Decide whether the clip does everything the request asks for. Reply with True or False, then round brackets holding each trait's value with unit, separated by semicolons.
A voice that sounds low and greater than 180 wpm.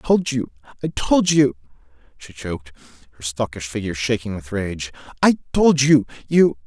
False (120 Hz; 145 wpm)